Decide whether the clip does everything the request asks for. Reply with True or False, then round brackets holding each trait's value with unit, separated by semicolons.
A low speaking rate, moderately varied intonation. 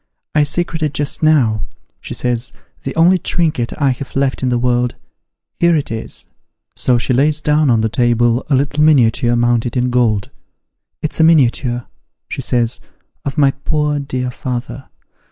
False (170 wpm; 3.8 semitones)